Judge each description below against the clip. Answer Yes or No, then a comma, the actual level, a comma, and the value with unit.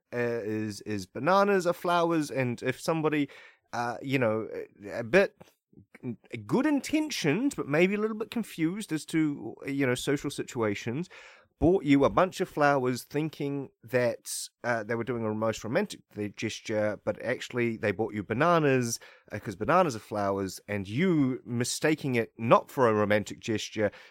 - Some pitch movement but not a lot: No, wide, 6.4 semitones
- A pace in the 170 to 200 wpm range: No, average, 160 wpm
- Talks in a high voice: No, low, 135 Hz